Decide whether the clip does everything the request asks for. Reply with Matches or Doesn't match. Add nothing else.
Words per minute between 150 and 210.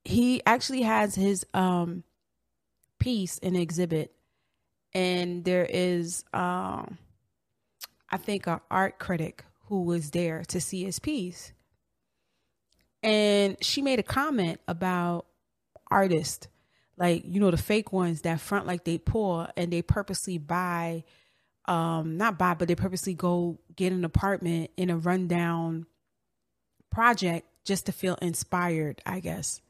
Doesn't match